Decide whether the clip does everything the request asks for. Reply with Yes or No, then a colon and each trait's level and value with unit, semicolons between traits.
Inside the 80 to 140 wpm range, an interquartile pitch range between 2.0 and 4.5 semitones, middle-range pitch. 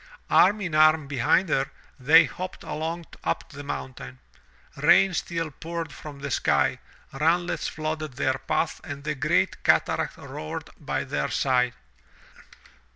Yes: slow, 135 wpm; average, 3.4 semitones; medium, 155 Hz